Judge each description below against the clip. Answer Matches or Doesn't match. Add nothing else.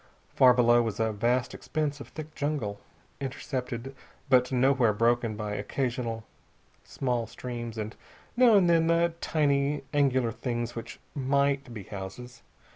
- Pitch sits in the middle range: Doesn't match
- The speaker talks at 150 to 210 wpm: Doesn't match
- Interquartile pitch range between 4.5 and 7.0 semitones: Doesn't match